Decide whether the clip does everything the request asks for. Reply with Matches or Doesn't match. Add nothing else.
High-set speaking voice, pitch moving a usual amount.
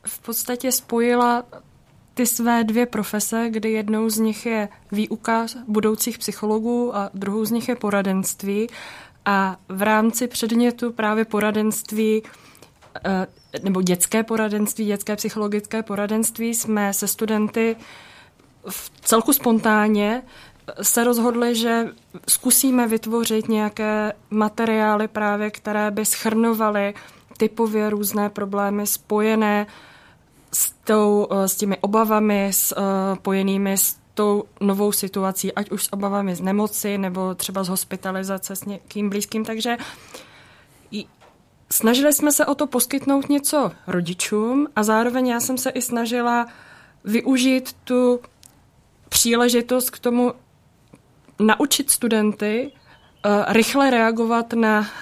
Doesn't match